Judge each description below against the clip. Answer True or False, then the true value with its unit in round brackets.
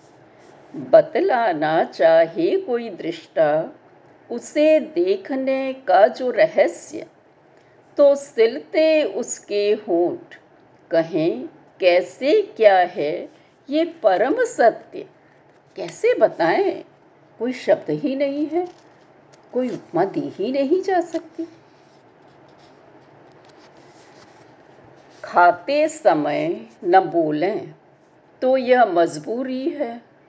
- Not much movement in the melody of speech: False (4.8 semitones)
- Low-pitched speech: False (310 Hz)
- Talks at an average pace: False (85 wpm)